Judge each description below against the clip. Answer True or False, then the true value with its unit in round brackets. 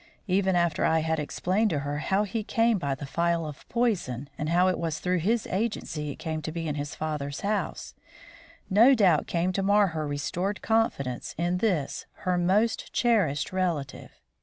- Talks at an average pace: True (185 wpm)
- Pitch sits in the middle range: True (175 Hz)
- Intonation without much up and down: False (4.9 semitones)